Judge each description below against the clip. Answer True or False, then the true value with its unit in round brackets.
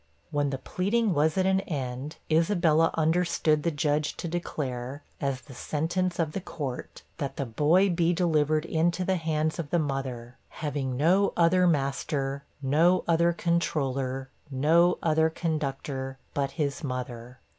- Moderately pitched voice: True (155 Hz)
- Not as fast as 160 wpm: True (145 wpm)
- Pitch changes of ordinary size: True (3.7 semitones)